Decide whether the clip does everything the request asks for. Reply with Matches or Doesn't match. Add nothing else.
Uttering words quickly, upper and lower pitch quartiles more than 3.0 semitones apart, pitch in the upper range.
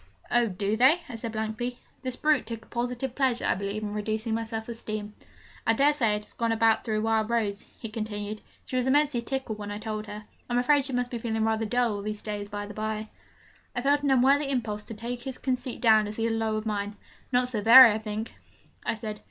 Doesn't match